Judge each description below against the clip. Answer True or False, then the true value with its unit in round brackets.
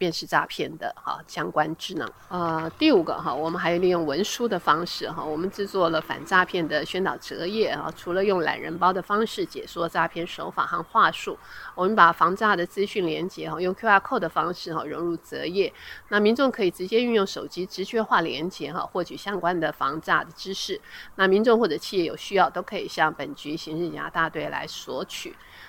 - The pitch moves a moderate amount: True (3.9 semitones)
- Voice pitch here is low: False (180 Hz)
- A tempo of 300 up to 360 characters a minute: True (320 characters per minute)